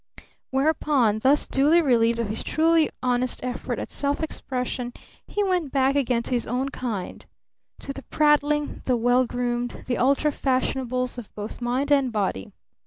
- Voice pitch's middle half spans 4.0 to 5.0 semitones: No, average, 2.8 semitones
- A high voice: Yes, very high, 255 Hz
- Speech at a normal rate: Yes, average, 160 wpm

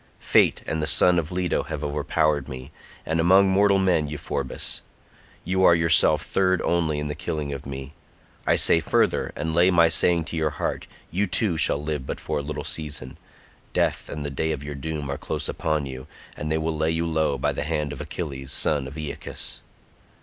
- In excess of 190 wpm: Yes, average, 200 wpm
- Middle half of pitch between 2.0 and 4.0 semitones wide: Yes, narrow, 2.5 semitones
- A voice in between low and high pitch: No, very low, 80 Hz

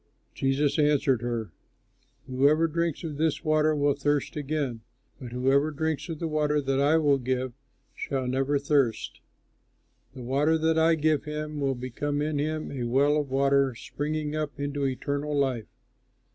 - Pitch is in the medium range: Yes, medium, 145 Hz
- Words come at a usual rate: Yes, average, 160 wpm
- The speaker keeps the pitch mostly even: Yes, narrow, 2.3 semitones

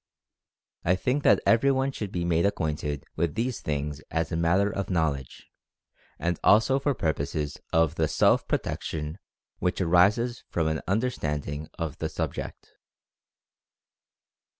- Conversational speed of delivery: No, slow, 130 wpm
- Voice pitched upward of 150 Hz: No, very low, 85 Hz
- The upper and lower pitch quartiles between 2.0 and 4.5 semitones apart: No, average, 5.1 semitones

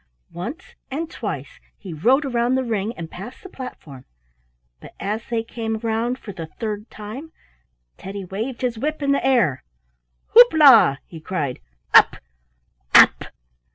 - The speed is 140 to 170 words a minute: Yes, average, 150 wpm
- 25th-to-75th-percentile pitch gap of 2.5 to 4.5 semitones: No, average, 5.3 semitones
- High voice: Yes, high, 225 Hz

